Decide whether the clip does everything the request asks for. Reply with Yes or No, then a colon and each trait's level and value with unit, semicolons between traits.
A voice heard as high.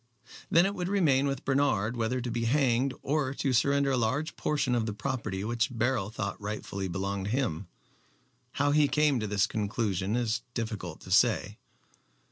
No: low, 120 Hz